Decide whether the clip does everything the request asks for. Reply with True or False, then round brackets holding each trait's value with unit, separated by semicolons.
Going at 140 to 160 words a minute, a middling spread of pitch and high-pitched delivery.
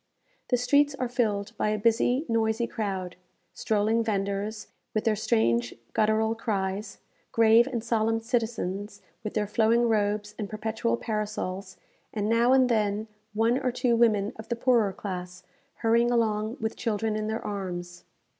False (150 wpm; 2.2 semitones; 220 Hz)